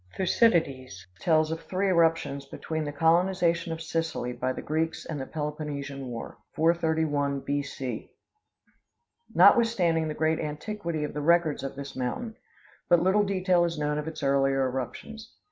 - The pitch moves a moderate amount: Yes, average, 3.3 semitones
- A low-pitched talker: No, medium, 160 Hz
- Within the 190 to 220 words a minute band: No, average, 150 wpm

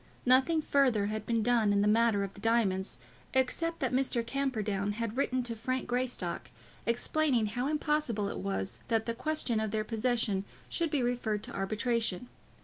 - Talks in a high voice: Yes, high, 230 Hz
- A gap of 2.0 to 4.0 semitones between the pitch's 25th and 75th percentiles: Yes, average, 3.6 semitones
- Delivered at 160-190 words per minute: Yes, average, 170 wpm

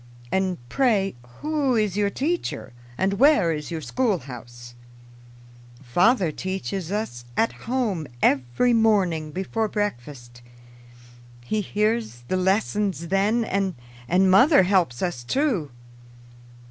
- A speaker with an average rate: No, slow, 110 wpm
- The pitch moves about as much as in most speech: No, wide, 6.1 semitones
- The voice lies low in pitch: No, high, 190 Hz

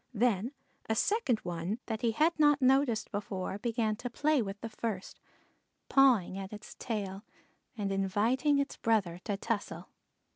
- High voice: Yes, high, 220 Hz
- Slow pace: No, average, 150 wpm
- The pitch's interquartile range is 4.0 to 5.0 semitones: Yes, average, 4.4 semitones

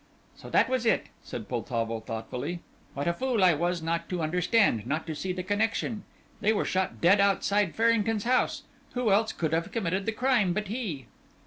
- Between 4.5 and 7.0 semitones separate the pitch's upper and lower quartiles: Yes, average, 5.2 semitones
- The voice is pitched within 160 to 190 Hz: Yes, medium, 185 Hz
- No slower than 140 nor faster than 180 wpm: No, average, 190 wpm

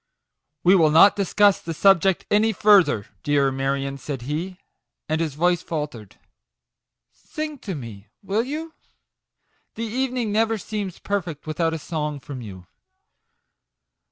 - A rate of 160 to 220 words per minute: No, average, 150 wpm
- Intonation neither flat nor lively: No, wide, 6.2 semitones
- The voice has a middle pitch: Yes, medium, 165 Hz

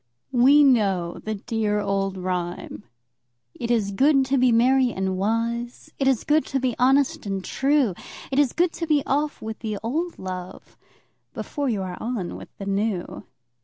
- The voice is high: Yes, high, 230 Hz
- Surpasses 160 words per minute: Yes, average, 170 wpm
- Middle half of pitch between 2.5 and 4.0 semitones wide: No, wide, 5.5 semitones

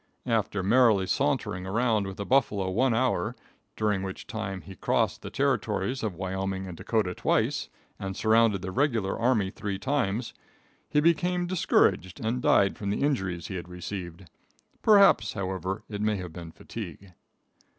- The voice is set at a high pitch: No, low, 100 Hz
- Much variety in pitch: No, average, 3.6 semitones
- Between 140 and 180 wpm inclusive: Yes, average, 155 wpm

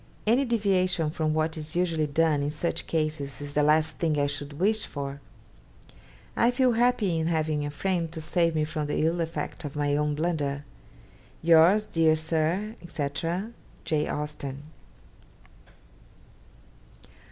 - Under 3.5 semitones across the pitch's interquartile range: Yes, average, 2.9 semitones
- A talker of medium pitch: Yes, medium, 160 Hz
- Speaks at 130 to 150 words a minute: Yes, average, 145 wpm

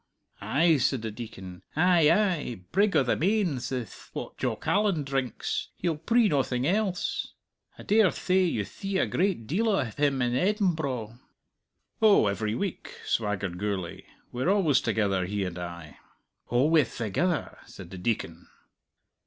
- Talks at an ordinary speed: Yes, average, 150 wpm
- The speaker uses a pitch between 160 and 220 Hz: No, low, 135 Hz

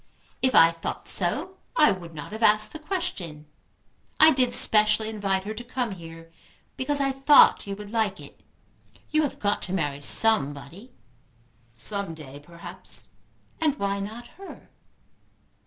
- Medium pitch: No, high, 210 Hz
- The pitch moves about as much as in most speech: No, wide, 7.4 semitones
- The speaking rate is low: No, average, 150 wpm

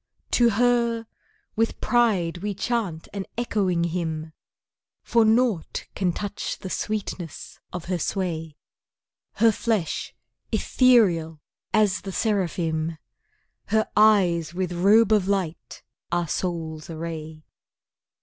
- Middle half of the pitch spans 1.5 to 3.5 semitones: No, average, 4.6 semitones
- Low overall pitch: No, medium, 185 Hz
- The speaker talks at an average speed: No, slow, 110 wpm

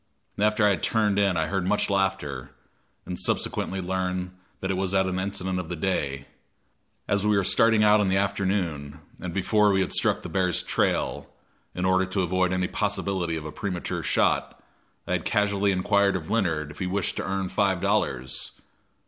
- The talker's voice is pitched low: Yes, very low, 95 Hz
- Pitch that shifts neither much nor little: No, narrow, 1.9 semitones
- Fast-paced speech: No, average, 190 wpm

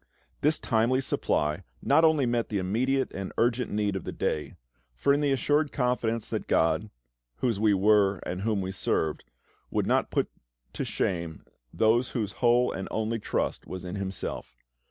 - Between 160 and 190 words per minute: Yes, average, 170 wpm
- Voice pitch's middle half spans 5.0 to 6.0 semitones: No, average, 4.5 semitones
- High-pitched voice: No, low, 110 Hz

